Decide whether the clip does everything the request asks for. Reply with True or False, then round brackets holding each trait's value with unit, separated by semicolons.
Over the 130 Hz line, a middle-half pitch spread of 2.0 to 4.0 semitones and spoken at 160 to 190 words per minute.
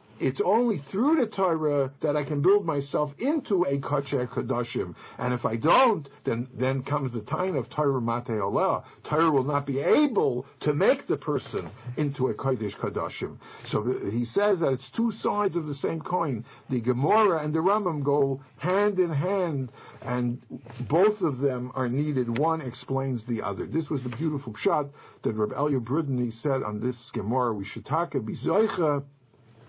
False (140 Hz; 4.4 semitones; 175 wpm)